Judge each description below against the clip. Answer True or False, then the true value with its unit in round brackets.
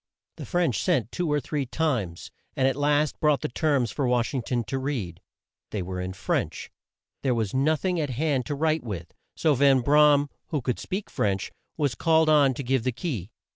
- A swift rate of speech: True (210 wpm)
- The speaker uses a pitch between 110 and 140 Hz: True (135 Hz)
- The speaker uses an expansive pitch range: False (4.2 semitones)